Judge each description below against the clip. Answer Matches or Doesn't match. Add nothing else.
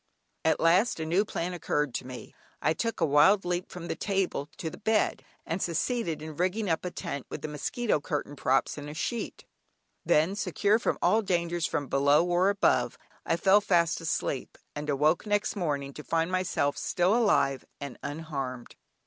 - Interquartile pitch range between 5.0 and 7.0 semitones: Doesn't match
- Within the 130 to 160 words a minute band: Doesn't match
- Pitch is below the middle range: Doesn't match